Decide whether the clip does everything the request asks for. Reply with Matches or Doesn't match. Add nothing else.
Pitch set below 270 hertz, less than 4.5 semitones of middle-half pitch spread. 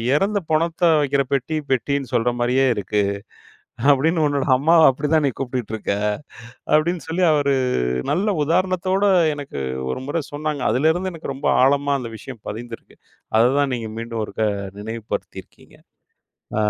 Doesn't match